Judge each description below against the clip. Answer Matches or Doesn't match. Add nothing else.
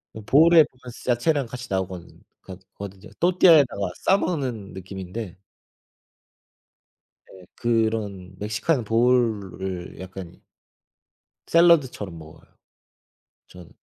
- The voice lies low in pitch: Matches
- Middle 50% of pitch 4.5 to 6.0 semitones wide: Matches